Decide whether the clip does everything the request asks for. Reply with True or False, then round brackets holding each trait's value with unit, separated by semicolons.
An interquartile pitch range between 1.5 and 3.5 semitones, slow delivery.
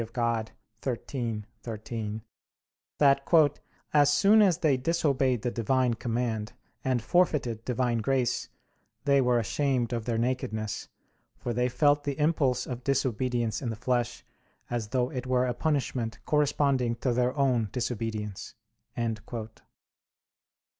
True (3.0 semitones; 125 wpm)